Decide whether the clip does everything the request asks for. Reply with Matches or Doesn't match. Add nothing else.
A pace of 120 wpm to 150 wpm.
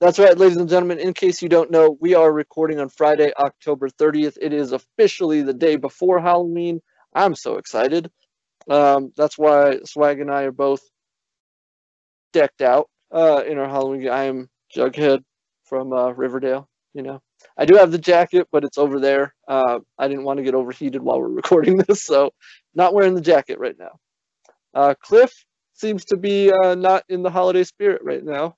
Doesn't match